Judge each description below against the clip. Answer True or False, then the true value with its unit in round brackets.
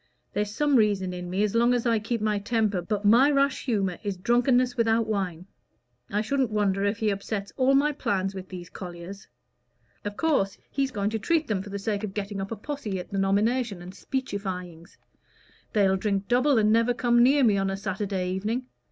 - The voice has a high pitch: True (210 Hz)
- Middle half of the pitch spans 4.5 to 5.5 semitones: False (3.7 semitones)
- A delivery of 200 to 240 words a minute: True (205 wpm)